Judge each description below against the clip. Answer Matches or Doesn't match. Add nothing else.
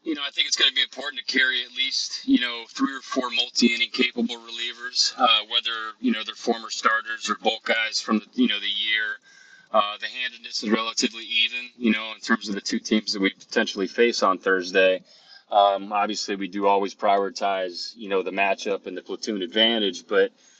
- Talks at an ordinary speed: Doesn't match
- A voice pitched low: Matches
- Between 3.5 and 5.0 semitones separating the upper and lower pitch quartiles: Matches